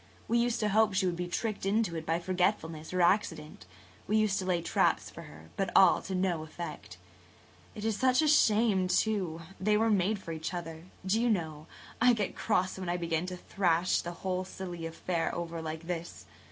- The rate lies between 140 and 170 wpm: No, fast, 205 wpm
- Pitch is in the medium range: Yes, medium, 180 Hz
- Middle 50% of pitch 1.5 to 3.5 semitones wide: No, average, 4.0 semitones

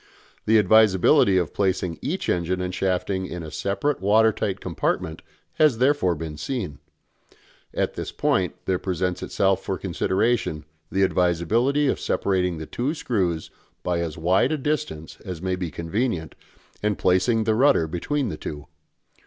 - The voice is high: No, very low, 95 Hz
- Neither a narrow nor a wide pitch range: Yes, average, 4.5 semitones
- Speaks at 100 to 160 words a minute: Yes, average, 155 wpm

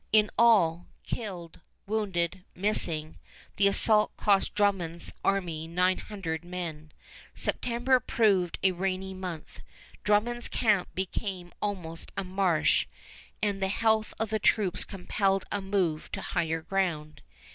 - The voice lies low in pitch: No, high, 190 Hz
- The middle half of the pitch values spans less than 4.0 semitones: Yes, average, 3.3 semitones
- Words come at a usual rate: No, slow, 125 wpm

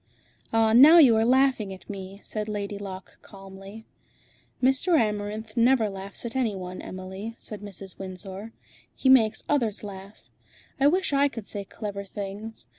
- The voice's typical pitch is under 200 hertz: No, high, 210 Hz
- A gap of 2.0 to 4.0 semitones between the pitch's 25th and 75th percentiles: Yes, average, 3.2 semitones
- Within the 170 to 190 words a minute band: No, average, 155 wpm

